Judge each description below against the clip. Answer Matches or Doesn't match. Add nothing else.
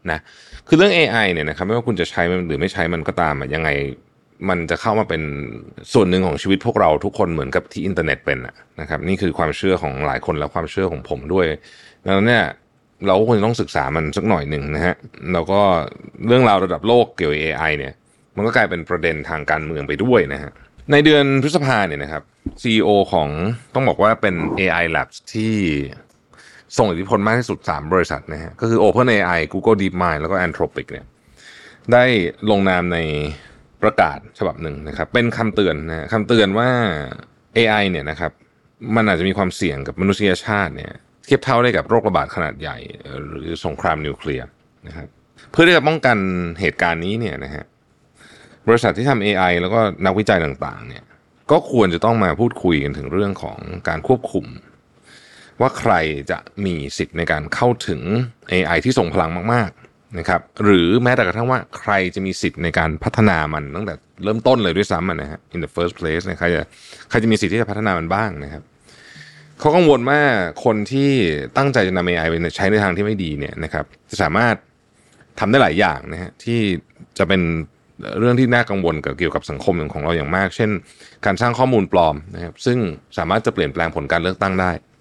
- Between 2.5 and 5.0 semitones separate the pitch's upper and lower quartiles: Doesn't match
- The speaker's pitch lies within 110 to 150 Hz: Doesn't match